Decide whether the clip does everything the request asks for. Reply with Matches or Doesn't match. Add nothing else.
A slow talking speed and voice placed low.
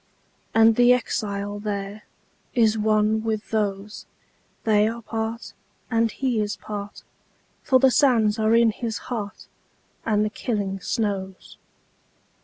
Doesn't match